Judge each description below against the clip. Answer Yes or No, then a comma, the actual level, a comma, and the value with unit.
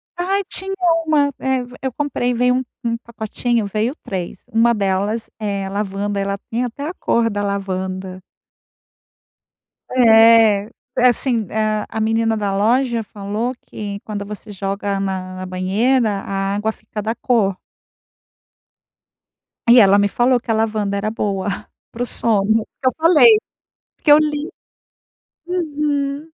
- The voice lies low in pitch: No, high, 220 Hz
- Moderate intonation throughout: Yes, average, 3.9 semitones